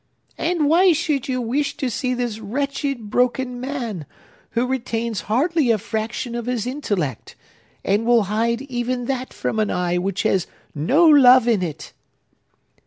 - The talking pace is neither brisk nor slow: Yes, average, 155 wpm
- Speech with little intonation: No, average, 3.9 semitones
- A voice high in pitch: Yes, high, 240 Hz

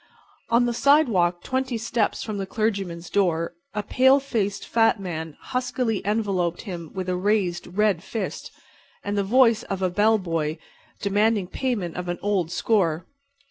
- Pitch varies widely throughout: No, average, 4.2 semitones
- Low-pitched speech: No, high, 200 Hz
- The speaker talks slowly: No, average, 155 wpm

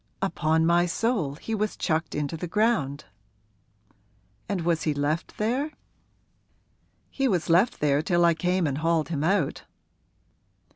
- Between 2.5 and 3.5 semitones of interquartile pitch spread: No, average, 4.4 semitones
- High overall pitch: No, medium, 170 Hz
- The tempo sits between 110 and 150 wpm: Yes, average, 140 wpm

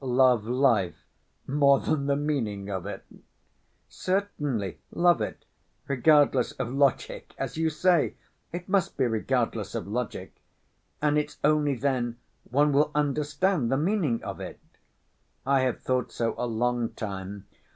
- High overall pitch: No, low, 135 Hz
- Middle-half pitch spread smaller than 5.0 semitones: Yes, average, 4.3 semitones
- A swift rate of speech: No, average, 140 wpm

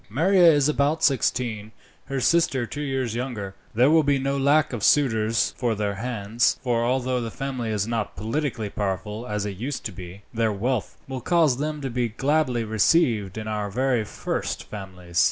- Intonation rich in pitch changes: No, average, 4.5 semitones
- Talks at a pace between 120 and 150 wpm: No, average, 180 wpm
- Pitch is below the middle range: Yes, low, 120 Hz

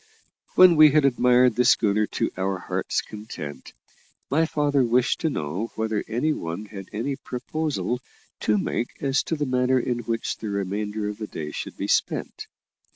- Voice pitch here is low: Yes, low, 115 Hz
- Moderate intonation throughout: Yes, average, 4.6 semitones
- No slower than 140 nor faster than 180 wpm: Yes, average, 170 wpm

